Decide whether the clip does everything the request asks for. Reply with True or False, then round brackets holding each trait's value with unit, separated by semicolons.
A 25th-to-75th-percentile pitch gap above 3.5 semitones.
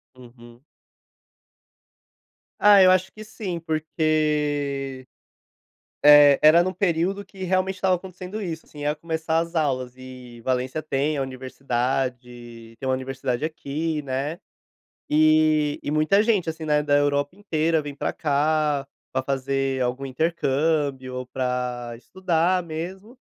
True (4.1 semitones)